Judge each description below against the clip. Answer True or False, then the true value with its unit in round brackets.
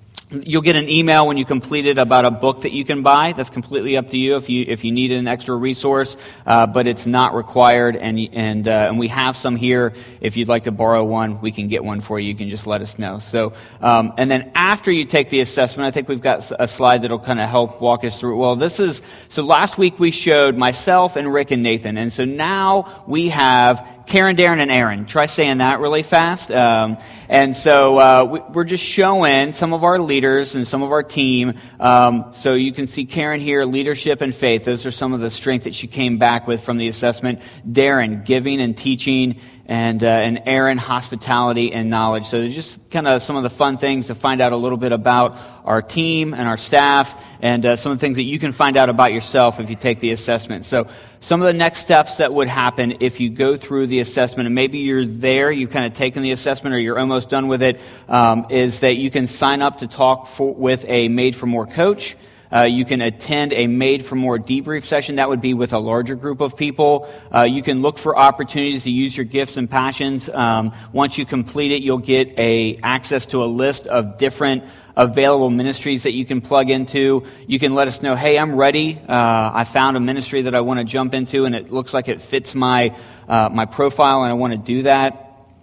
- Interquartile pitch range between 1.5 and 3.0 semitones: True (2.6 semitones)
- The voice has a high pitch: False (130 Hz)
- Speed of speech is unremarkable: False (235 wpm)